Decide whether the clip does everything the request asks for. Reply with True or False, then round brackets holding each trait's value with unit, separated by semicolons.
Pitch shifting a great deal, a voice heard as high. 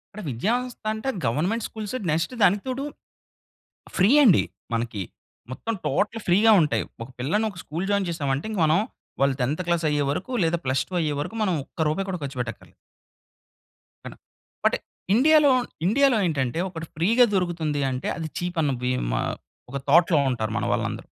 False (6.7 semitones; 170 Hz)